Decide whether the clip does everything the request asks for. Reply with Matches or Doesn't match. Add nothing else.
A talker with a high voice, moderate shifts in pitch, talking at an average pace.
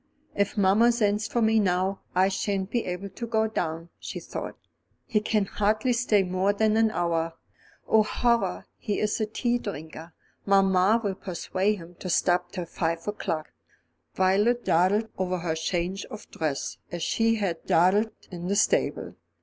Matches